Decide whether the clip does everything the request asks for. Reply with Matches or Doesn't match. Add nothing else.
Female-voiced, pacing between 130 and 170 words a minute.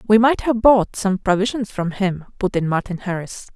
Doesn't match